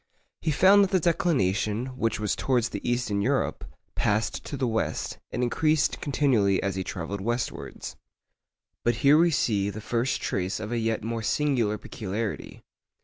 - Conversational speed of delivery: Yes, average, 165 wpm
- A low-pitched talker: Yes, low, 115 Hz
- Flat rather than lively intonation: No, average, 4.9 semitones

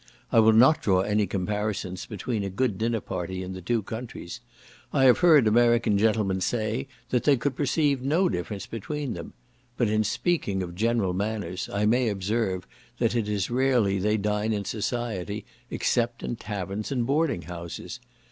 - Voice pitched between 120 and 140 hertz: No, low, 110 Hz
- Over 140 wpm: Yes, average, 170 wpm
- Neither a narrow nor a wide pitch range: Yes, average, 3.6 semitones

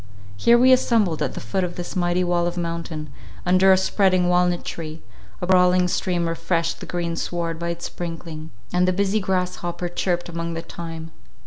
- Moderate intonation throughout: No, narrow, 1.6 semitones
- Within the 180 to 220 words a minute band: Yes, average, 185 wpm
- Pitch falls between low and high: Yes, medium, 175 Hz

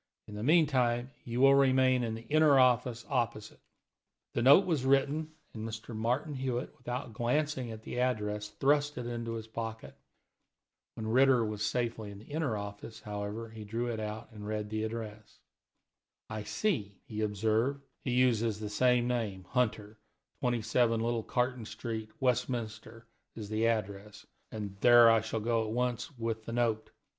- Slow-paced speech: No, average, 160 wpm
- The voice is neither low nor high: No, low, 115 Hz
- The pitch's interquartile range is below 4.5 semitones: Yes, narrow, 2.6 semitones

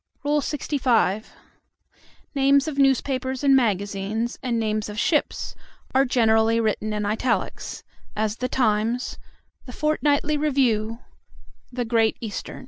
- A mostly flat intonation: No, average, 4.0 semitones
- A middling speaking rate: No, slow, 120 wpm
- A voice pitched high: Yes, high, 240 Hz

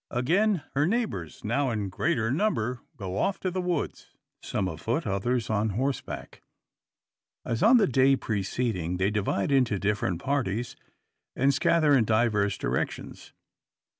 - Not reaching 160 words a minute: Yes, slow, 135 wpm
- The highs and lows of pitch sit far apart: Yes, wide, 5.8 semitones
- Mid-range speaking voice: No, low, 120 Hz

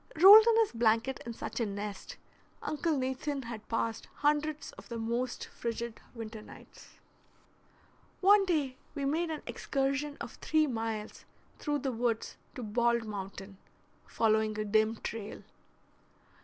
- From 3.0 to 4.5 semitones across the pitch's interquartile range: No, average, 4.9 semitones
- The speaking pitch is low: No, high, 235 Hz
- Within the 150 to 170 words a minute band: No, average, 140 wpm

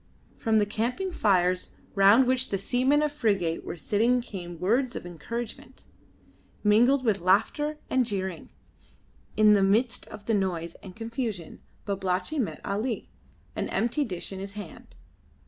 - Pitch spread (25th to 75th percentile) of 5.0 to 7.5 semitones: No, average, 4.5 semitones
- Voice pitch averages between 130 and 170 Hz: No, high, 210 Hz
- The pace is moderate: Yes, average, 150 wpm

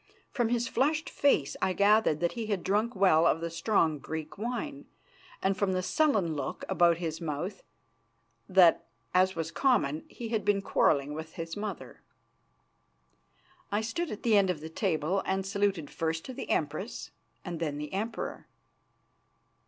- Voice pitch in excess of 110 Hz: Yes, high, 190 Hz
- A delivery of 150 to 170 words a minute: Yes, average, 160 wpm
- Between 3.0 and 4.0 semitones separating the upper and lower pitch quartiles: No, average, 5.0 semitones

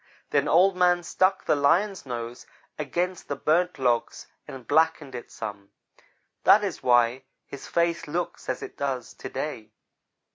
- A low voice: No, medium, 150 Hz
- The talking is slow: No, average, 150 wpm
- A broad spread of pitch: Yes, wide, 5.8 semitones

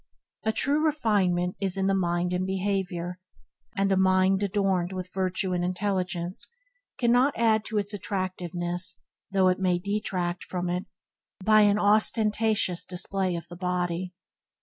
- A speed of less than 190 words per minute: Yes, average, 145 wpm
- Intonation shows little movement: Yes, narrow, 2.3 semitones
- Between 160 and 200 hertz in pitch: Yes, high, 190 Hz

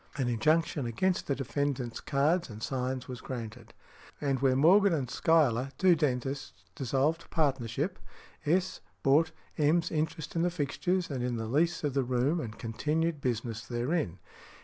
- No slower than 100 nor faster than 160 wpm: Yes, average, 155 wpm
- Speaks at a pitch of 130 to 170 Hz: Yes, medium, 140 Hz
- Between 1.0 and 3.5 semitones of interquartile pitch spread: No, average, 4.7 semitones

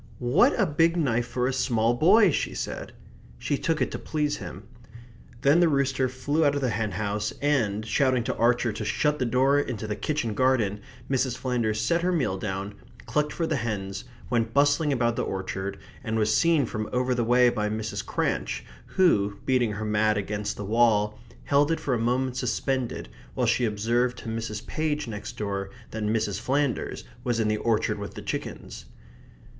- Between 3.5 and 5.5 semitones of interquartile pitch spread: Yes, average, 4.6 semitones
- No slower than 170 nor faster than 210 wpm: Yes, average, 190 wpm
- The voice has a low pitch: Yes, low, 120 Hz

